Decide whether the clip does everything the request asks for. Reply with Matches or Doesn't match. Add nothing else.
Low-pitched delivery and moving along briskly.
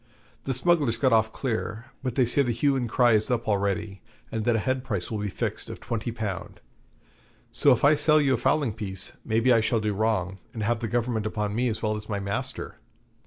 Matches